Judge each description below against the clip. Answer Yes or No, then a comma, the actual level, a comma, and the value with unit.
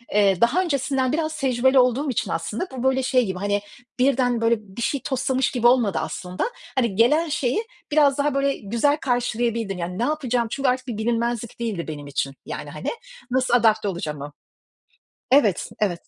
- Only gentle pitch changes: No, average, 4.2 semitones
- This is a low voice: No, high, 240 Hz